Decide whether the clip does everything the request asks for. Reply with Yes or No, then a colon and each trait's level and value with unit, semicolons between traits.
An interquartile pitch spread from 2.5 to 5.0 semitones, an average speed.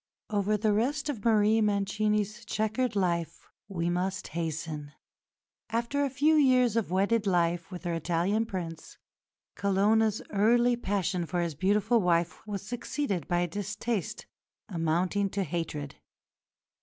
No: average, 4.2 semitones; slow, 130 wpm